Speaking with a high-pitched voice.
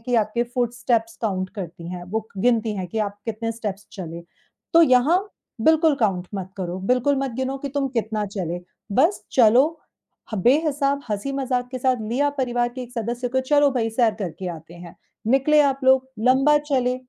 Yes: high, 240 Hz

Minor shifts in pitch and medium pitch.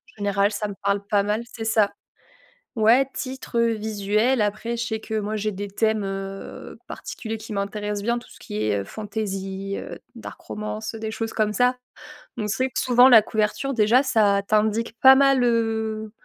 No: narrow, 2.1 semitones; high, 215 Hz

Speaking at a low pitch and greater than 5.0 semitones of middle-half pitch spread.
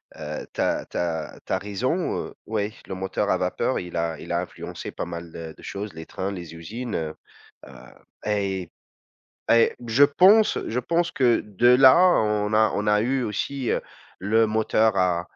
Yes: low, 105 Hz; wide, 5.5 semitones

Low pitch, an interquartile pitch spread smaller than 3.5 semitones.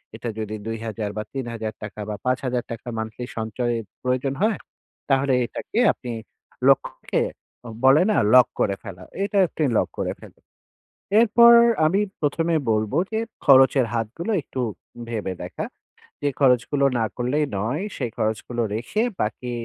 No: low, 125 Hz; average, 3.9 semitones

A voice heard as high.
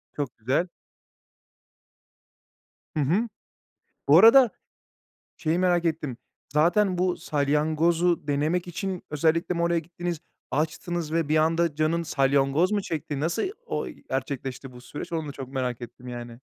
No: medium, 160 Hz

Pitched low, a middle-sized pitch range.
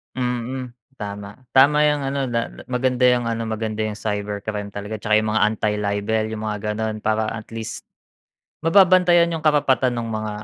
Yes: low, 110 Hz; average, 3.4 semitones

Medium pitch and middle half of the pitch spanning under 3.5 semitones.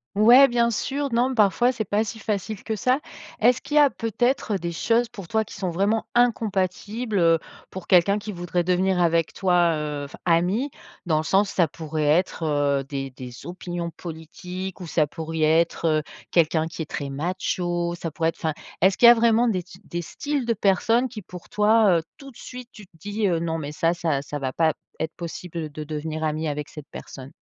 No: medium, 180 Hz; average, 5.3 semitones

